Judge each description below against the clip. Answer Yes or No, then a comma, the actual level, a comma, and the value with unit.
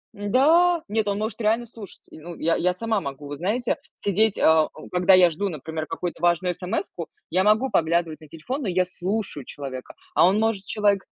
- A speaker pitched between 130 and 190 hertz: Yes, medium, 185 Hz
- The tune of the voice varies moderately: Yes, average, 4.6 semitones